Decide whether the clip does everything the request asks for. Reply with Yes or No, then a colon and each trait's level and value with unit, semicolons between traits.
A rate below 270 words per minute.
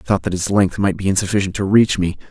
No: fast, 285 wpm